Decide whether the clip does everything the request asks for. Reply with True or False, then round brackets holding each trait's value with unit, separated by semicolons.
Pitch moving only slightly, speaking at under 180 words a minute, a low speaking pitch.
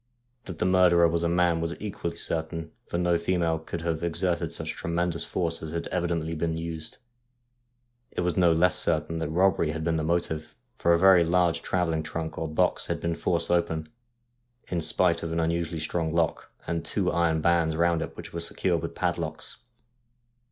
False (1.1 semitones; 190 wpm; 85 Hz)